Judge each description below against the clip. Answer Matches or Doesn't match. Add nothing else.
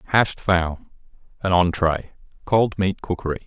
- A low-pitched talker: Matches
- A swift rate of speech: Doesn't match